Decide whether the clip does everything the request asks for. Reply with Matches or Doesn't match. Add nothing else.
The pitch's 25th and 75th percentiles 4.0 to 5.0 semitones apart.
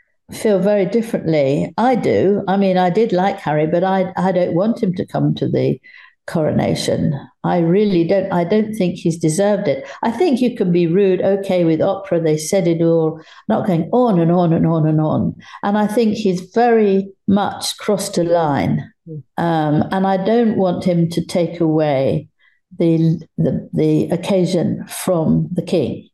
Doesn't match